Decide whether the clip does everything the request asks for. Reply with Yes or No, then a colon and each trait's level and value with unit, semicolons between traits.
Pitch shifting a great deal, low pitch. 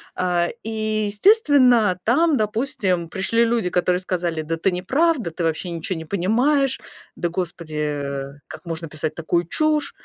No: wide, 5.9 semitones; medium, 185 Hz